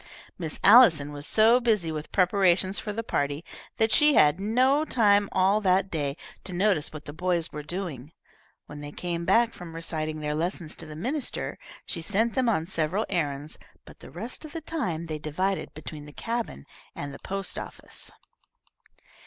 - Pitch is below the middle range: No, medium, 180 Hz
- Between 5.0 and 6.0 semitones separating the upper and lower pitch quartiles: Yes, wide, 5.6 semitones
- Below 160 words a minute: No, average, 180 wpm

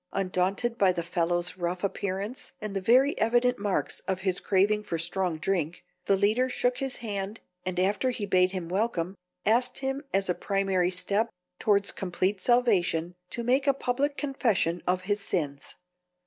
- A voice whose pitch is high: Yes, high, 195 Hz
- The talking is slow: No, average, 165 wpm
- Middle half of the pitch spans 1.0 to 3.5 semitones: No, average, 4.3 semitones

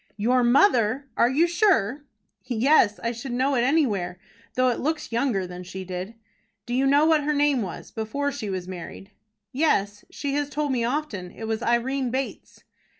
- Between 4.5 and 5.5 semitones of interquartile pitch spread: Yes, average, 5.2 semitones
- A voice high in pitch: Yes, high, 245 Hz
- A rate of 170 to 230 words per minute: Yes, average, 180 wpm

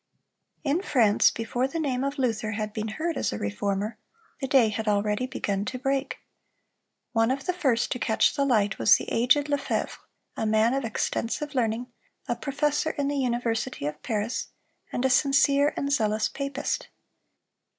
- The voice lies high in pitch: Yes, very high, 250 Hz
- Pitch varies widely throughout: No, average, 4.2 semitones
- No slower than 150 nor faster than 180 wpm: Yes, average, 170 wpm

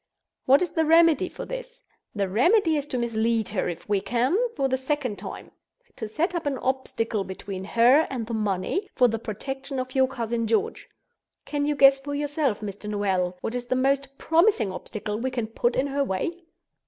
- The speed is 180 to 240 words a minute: Yes, average, 190 wpm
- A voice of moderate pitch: No, very high, 255 Hz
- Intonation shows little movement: No, average, 4.9 semitones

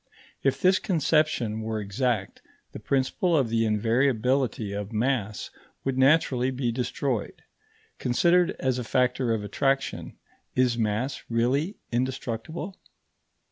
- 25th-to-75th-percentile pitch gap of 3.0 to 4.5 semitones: Yes, average, 3.4 semitones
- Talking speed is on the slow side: Yes, slow, 115 wpm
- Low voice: Yes, low, 125 Hz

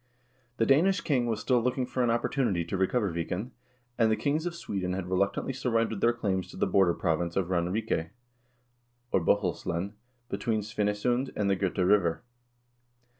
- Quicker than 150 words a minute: Yes, average, 165 wpm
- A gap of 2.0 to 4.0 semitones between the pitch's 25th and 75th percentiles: No, average, 4.8 semitones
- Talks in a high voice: No, low, 105 Hz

